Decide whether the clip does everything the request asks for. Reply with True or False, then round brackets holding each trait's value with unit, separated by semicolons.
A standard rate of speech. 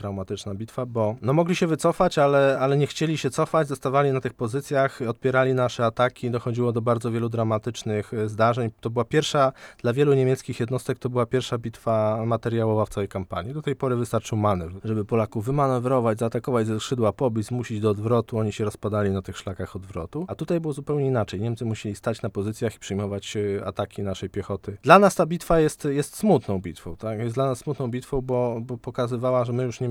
False (200 wpm)